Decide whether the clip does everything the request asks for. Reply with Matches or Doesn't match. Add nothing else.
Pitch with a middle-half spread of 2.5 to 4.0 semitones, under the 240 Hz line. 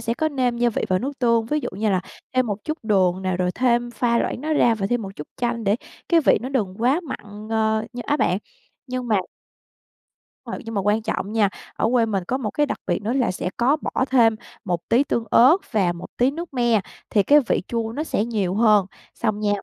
Matches